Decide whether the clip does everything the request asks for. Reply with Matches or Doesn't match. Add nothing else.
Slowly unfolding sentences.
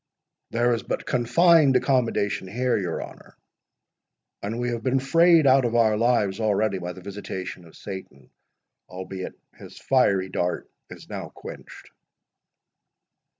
Matches